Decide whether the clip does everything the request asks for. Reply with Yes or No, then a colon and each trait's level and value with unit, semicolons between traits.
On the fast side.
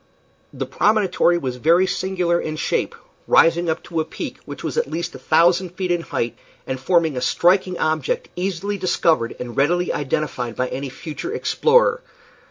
No: average, 170 wpm